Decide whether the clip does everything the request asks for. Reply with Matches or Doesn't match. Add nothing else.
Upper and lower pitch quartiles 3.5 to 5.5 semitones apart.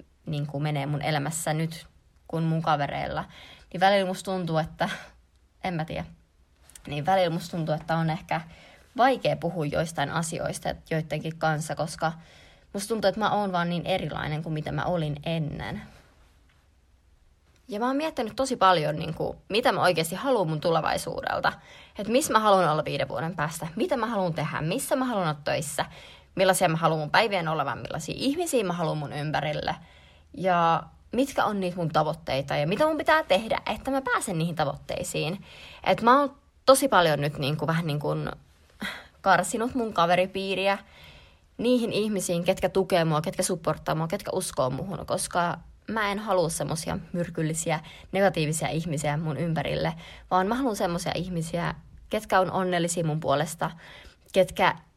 Matches